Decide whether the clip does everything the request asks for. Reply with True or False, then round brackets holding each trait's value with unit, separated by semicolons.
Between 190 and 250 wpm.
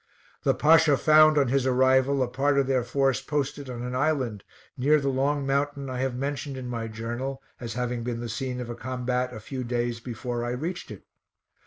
True (205 wpm)